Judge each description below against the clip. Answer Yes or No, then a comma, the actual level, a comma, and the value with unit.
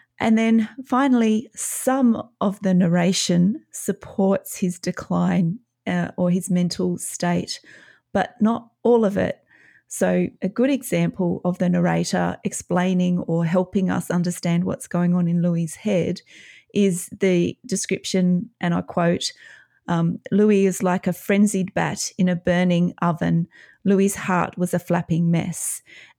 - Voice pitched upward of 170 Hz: Yes, medium, 185 Hz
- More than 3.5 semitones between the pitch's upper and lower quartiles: No, narrow, 2.6 semitones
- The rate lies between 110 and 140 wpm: Yes, slow, 135 wpm